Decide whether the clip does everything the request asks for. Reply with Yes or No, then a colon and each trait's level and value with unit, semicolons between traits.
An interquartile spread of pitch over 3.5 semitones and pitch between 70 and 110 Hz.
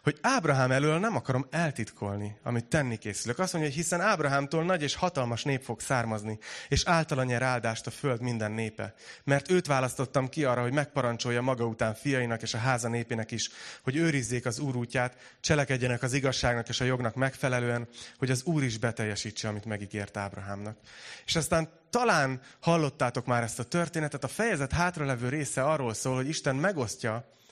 No: average, 4.0 semitones; low, 130 Hz